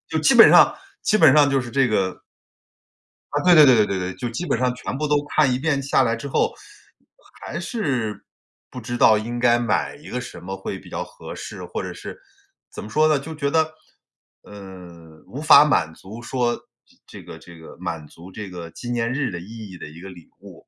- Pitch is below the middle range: Yes, low, 120 Hz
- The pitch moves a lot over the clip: Yes, wide, 6.8 semitones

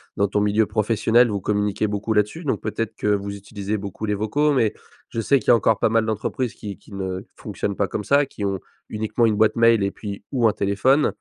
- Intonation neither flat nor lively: No, narrow, 2.1 semitones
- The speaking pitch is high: No, low, 105 Hz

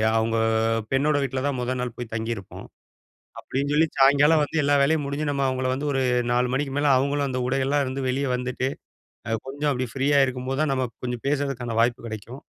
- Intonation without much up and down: Yes, narrow, 2.3 semitones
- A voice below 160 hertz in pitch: Yes, low, 135 Hz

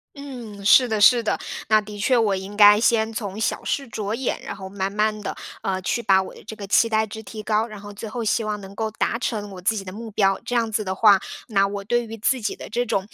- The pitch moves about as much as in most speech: No, narrow, 2.1 semitones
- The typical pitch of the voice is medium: No, high, 215 Hz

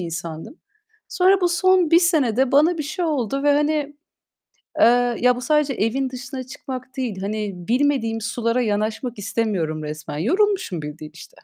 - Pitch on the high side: Yes, very high, 250 Hz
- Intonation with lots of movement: Yes, wide, 5.7 semitones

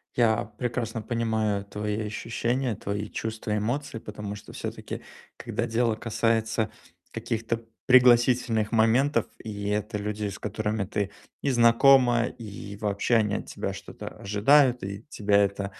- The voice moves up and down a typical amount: No, narrow, 2.2 semitones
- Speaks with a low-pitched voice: Yes, low, 110 Hz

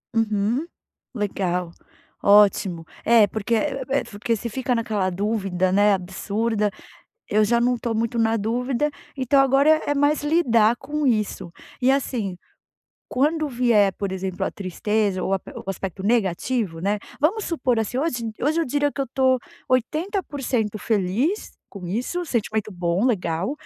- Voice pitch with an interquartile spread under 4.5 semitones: No, average, 4.9 semitones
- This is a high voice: Yes, high, 225 Hz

